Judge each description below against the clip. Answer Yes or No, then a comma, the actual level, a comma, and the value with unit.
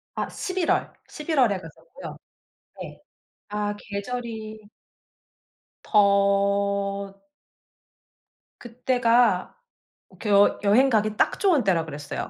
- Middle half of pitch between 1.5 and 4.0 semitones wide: Yes, average, 3.5 semitones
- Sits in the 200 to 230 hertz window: Yes, high, 210 Hz